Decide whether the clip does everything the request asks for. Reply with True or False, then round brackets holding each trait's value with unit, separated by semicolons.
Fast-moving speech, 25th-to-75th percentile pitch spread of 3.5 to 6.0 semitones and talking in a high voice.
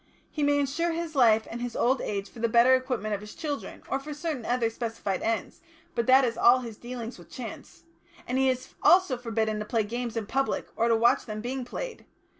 False (225 wpm; 3.0 semitones; 240 Hz)